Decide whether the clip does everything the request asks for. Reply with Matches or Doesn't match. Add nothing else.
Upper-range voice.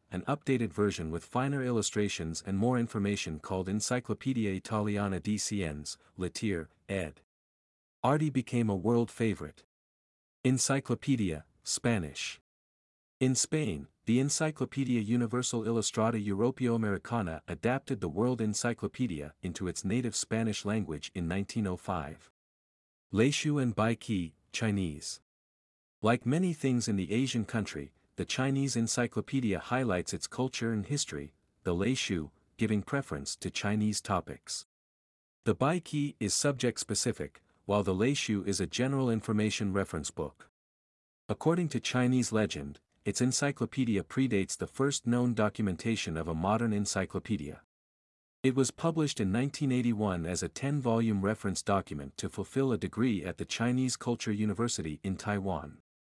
Doesn't match